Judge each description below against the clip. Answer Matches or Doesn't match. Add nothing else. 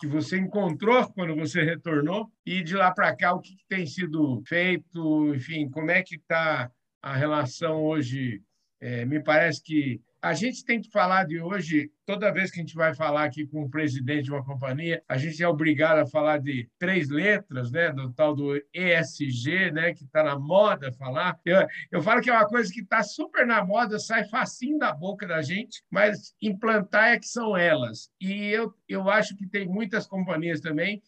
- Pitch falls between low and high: Matches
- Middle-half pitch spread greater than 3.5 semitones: Matches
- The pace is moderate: Doesn't match